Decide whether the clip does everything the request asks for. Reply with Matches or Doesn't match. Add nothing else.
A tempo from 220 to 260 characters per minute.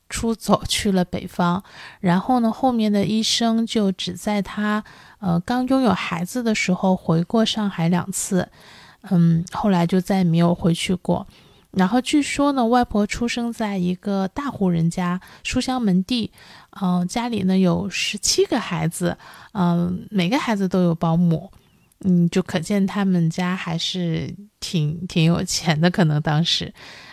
Matches